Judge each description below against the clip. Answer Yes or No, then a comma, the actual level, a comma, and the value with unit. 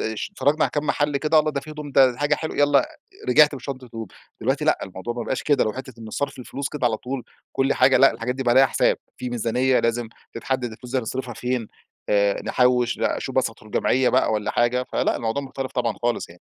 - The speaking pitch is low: Yes, low, 130 Hz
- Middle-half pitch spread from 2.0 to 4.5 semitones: Yes, average, 2.8 semitones